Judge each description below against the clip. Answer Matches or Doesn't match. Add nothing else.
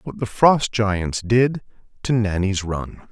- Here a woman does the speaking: Doesn't match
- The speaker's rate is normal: Matches